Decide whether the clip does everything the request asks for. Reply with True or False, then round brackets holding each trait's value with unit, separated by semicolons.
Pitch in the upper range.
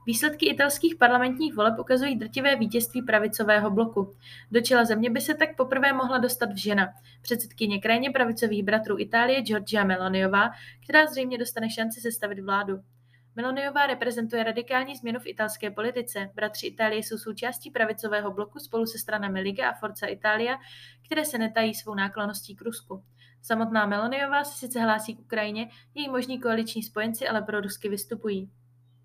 True (225 Hz)